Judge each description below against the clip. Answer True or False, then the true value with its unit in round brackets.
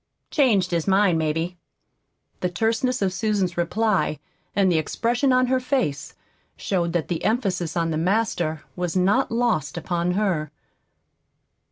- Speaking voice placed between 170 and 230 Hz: True (185 Hz)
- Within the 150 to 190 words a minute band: False (140 wpm)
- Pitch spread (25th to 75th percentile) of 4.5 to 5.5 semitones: True (4.9 semitones)